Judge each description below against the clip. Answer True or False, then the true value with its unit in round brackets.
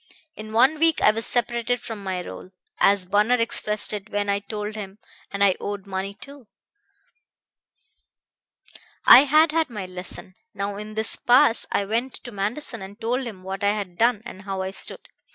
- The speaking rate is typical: True (180 wpm)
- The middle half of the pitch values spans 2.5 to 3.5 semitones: True (3.2 semitones)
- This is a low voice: False (210 Hz)